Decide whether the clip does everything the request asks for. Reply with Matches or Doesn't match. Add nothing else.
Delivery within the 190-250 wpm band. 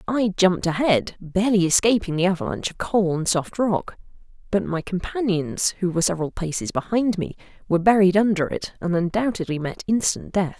Doesn't match